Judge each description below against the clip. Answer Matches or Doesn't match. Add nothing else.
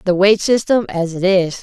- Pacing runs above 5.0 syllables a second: Doesn't match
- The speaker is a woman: Matches